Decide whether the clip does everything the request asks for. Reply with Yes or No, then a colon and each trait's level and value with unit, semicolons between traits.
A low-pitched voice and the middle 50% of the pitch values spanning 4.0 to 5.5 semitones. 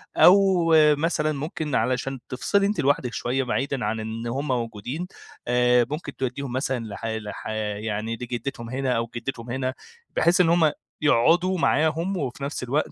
Yes: low, 130 Hz; average, 4.5 semitones